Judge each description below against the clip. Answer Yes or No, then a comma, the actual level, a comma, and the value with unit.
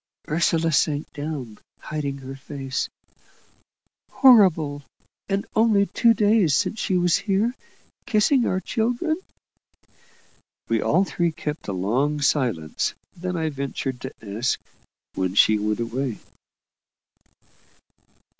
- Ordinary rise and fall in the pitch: No, wide, 7.0 semitones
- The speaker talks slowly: Yes, slow, 110 wpm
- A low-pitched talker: No, medium, 150 Hz